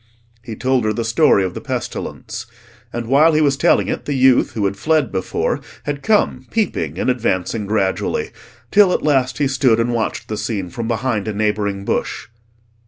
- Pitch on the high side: No, low, 120 Hz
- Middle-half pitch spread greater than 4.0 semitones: Yes, average, 4.7 semitones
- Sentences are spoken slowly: No, average, 185 wpm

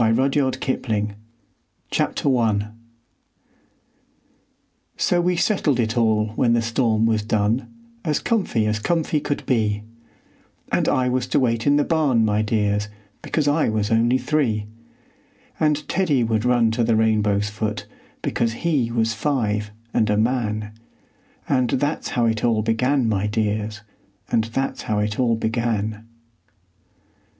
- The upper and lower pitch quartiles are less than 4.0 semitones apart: Yes, average, 3.4 semitones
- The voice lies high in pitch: No, low, 115 Hz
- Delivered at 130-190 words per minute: Yes, average, 140 wpm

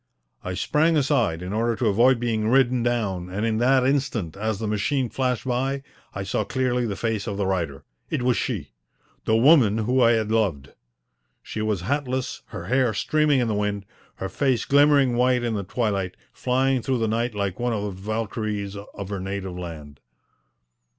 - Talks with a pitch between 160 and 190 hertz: No, low, 115 Hz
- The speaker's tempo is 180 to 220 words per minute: Yes, average, 185 wpm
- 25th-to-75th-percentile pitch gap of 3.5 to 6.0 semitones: Yes, average, 4.1 semitones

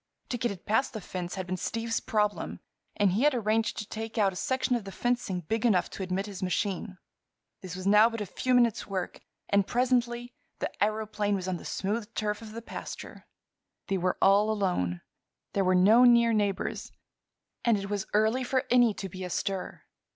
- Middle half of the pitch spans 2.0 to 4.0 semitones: Yes, average, 3.4 semitones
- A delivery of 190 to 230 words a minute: Yes, average, 195 wpm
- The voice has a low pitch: No, high, 210 Hz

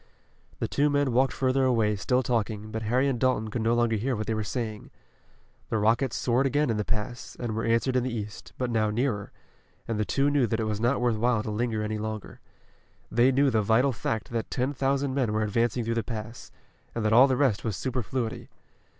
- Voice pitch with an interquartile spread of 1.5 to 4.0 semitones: Yes, average, 2.9 semitones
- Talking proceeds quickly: Yes, fast, 225 wpm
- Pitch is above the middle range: No, low, 115 Hz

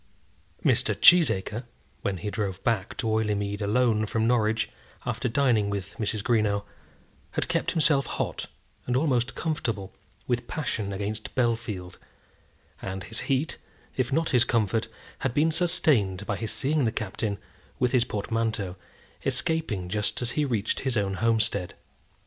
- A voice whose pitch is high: No, low, 110 Hz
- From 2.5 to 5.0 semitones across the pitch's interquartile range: Yes, average, 3.7 semitones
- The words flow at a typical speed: Yes, average, 145 wpm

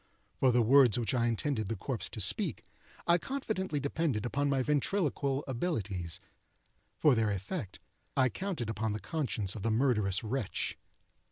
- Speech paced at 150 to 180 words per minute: Yes, average, 155 wpm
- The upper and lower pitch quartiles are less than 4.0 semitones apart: No, average, 5.2 semitones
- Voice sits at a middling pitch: No, low, 125 Hz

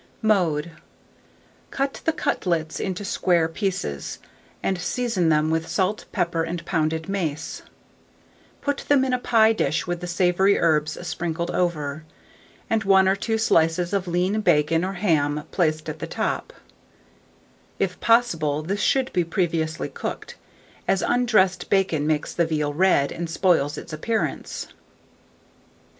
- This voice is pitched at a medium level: Yes, medium, 175 Hz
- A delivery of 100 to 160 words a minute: Yes, average, 140 wpm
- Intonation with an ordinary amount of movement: Yes, average, 3.7 semitones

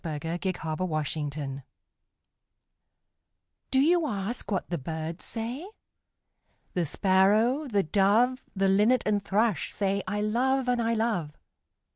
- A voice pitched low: No, high, 200 Hz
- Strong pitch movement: Yes, wide, 5.9 semitones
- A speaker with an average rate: No, slow, 130 wpm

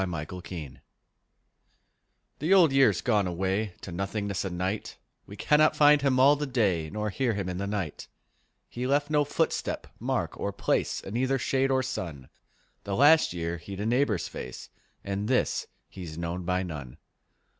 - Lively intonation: Yes, wide, 6.6 semitones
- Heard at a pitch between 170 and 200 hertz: No, low, 100 Hz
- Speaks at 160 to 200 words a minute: Yes, average, 170 wpm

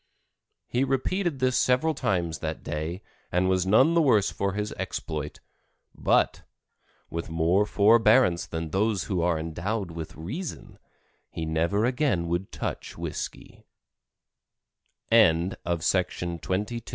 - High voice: No, very low, 95 Hz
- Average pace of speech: No, slow, 125 wpm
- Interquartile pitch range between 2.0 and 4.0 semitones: No, wide, 5.5 semitones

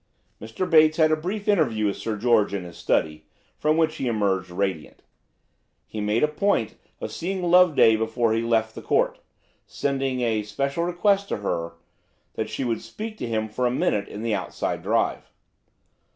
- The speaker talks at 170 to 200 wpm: Yes, average, 180 wpm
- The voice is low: Yes, low, 115 Hz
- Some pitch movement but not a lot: No, wide, 6.7 semitones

